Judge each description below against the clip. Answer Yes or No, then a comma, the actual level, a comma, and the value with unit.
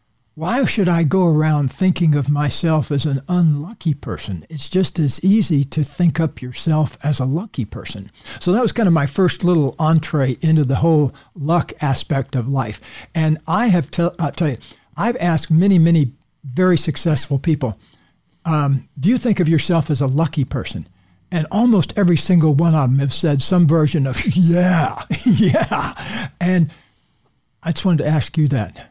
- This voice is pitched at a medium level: Yes, medium, 155 Hz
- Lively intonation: No, average, 4.0 semitones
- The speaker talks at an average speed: Yes, average, 175 wpm